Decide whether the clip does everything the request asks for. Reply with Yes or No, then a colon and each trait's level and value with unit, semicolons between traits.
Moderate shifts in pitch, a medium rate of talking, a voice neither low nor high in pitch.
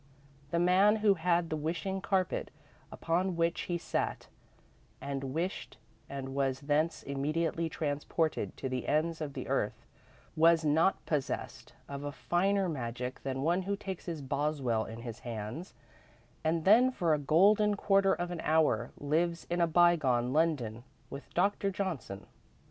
Yes: average, 4.3 semitones; average, 150 wpm; medium, 160 Hz